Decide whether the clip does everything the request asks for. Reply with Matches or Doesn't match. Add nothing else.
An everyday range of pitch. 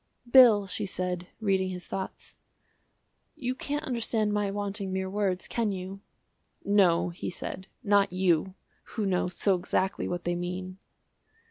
Doesn't match